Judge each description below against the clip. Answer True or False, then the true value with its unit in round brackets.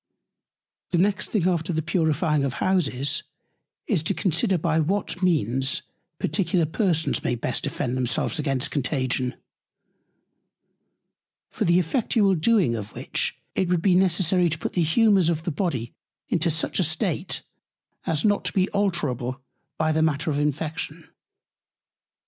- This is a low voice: False (160 Hz)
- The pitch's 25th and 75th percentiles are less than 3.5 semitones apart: False (3.9 semitones)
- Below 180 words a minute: True (145 wpm)